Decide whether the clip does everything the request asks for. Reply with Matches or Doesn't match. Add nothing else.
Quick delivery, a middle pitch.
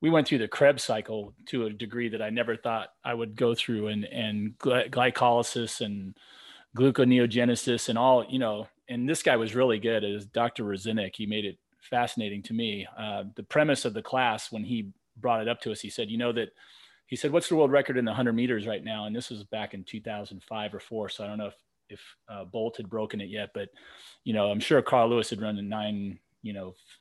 Doesn't match